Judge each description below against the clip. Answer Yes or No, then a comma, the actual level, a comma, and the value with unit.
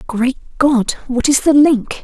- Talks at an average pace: Yes, average, 175 wpm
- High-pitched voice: Yes, very high, 260 Hz